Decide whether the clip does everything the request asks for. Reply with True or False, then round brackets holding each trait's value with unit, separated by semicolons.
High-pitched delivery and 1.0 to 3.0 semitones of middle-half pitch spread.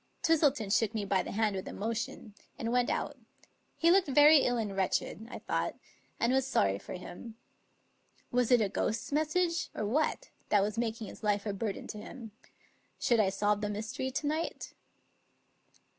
False (225 Hz; 4.4 semitones)